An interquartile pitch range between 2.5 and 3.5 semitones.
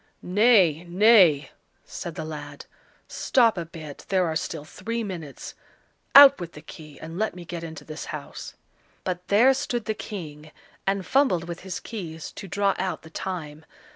No: average, 4.3 semitones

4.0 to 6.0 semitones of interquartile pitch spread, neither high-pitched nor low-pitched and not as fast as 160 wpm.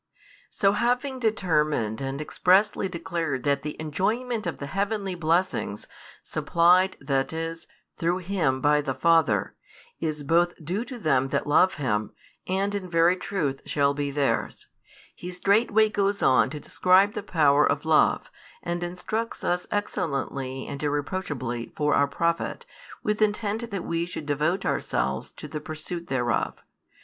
Yes: average, 5.3 semitones; medium, 170 Hz; average, 150 wpm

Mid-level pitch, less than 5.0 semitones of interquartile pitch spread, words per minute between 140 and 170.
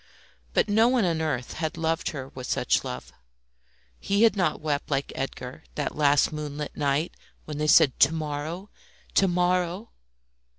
Yes: medium, 155 Hz; average, 3.6 semitones; average, 160 wpm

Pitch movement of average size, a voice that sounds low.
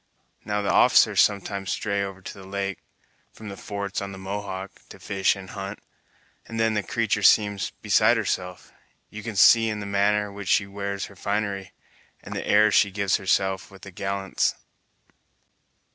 No: narrow, 1.1 semitones; low, 100 Hz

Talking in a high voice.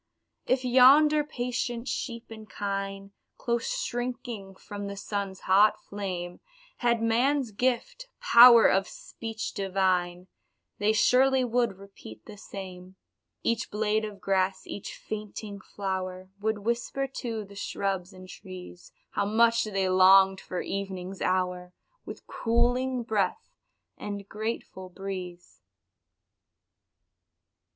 Yes: high, 205 Hz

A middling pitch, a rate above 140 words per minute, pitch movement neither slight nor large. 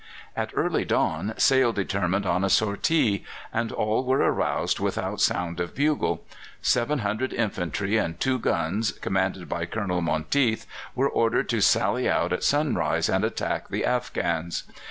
No: low, 100 Hz; average, 150 wpm; average, 5.0 semitones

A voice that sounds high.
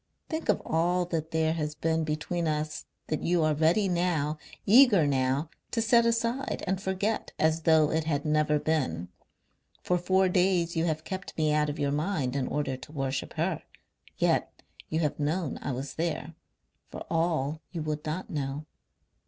No: medium, 160 Hz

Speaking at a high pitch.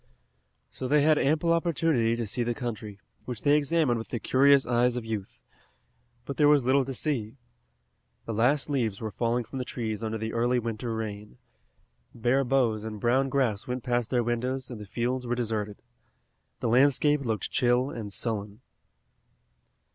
No: low, 120 Hz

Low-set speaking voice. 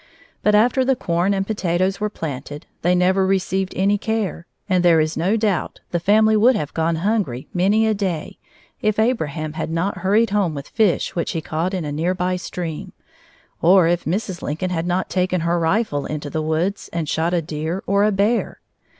No: medium, 180 Hz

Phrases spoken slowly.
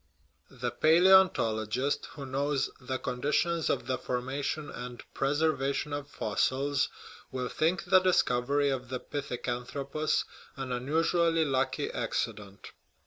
Yes: slow, 125 wpm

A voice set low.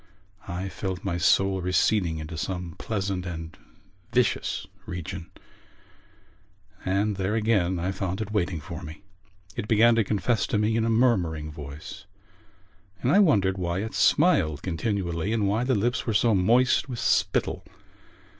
Yes: very low, 95 Hz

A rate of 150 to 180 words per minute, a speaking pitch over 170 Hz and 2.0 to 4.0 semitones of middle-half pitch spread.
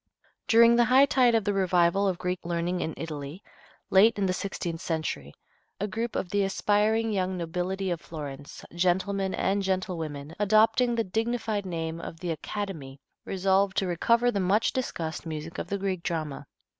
Yes: average, 170 wpm; high, 190 Hz; average, 3.7 semitones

